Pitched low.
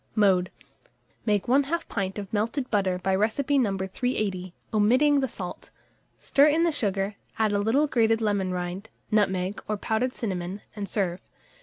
No: high, 210 Hz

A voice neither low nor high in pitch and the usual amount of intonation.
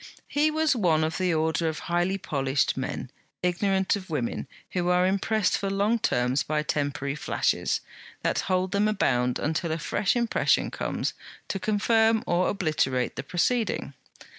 Yes: medium, 180 Hz; average, 4.7 semitones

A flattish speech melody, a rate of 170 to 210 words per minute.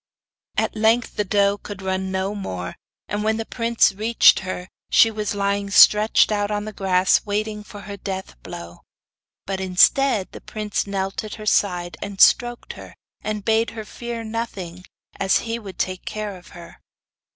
Yes: narrow, 2.3 semitones; average, 175 wpm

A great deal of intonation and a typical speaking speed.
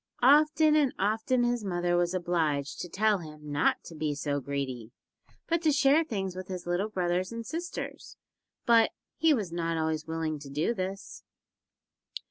Yes: wide, 6.9 semitones; average, 165 wpm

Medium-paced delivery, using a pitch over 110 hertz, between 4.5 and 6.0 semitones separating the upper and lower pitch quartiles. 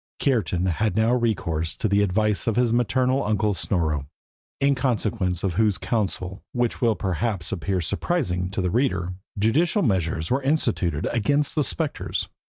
No: average, 155 wpm; low, 105 Hz; average, 5.1 semitones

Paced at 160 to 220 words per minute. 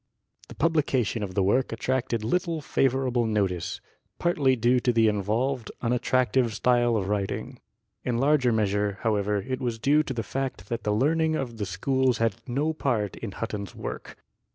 Yes: average, 165 wpm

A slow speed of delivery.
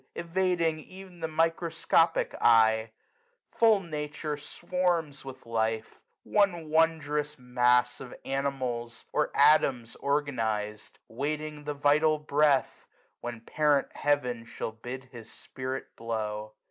Yes: slow, 110 wpm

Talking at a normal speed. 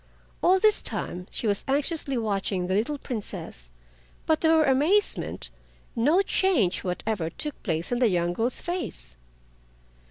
Yes: average, 145 wpm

